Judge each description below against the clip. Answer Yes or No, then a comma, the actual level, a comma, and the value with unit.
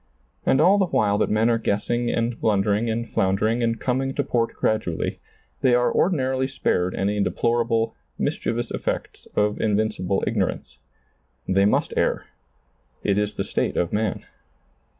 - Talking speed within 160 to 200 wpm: No, average, 150 wpm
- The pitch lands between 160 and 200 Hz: No, low, 115 Hz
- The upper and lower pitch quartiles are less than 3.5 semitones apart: Yes, average, 2.8 semitones